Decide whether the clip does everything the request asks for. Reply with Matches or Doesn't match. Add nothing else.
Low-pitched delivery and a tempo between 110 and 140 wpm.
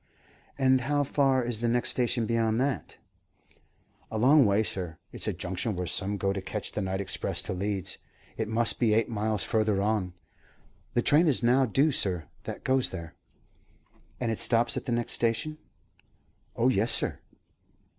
Doesn't match